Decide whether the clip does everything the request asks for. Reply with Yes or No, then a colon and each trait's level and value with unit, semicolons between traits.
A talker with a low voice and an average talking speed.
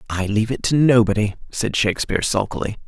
Yes: low, 110 Hz; average, 165 wpm